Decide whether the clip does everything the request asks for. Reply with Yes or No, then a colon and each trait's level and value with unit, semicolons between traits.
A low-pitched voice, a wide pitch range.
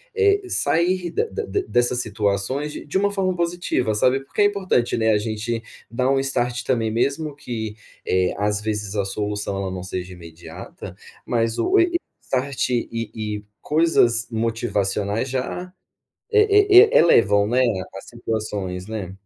Yes: low, 120 Hz; wide, 7.0 semitones